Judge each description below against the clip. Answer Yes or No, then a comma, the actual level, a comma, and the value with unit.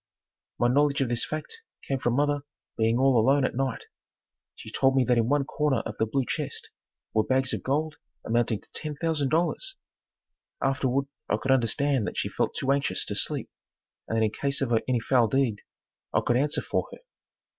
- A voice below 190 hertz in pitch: Yes, low, 135 Hz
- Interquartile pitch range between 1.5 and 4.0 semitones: Yes, average, 2.9 semitones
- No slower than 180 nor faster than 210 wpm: Yes, average, 190 wpm